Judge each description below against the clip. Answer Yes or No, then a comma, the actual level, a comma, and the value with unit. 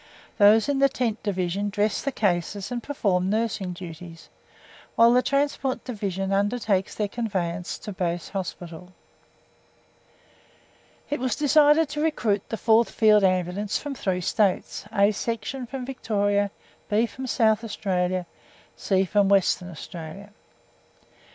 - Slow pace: Yes, slow, 130 wpm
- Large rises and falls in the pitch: No, average, 4.2 semitones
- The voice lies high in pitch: Yes, high, 205 Hz